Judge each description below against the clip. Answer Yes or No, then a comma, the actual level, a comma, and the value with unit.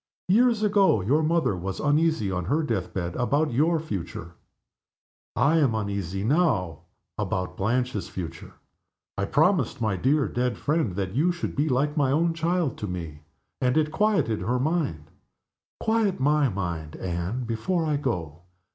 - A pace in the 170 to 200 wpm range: No, average, 155 wpm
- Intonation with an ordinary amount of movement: No, wide, 8.8 semitones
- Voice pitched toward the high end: No, low, 125 Hz